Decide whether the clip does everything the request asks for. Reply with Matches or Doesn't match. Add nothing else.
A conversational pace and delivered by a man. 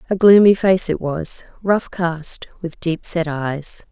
Doesn't match